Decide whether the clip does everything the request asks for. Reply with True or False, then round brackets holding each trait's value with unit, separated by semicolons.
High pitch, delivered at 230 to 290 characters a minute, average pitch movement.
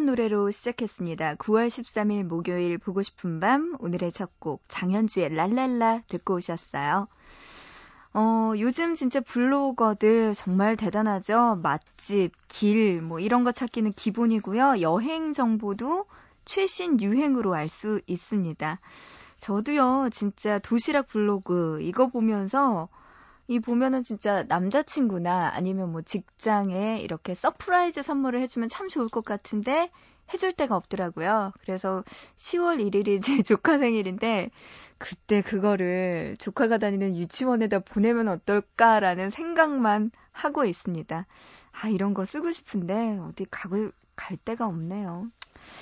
True (215 Hz; 280 characters per minute; 4.5 semitones)